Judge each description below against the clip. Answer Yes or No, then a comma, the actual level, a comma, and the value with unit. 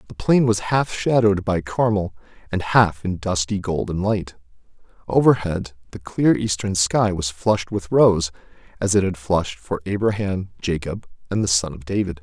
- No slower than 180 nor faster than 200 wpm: No, average, 165 wpm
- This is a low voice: Yes, very low, 95 Hz